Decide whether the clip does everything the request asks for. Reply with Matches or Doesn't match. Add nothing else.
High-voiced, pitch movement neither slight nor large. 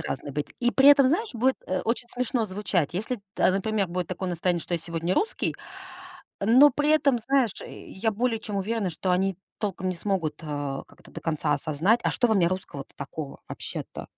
Doesn't match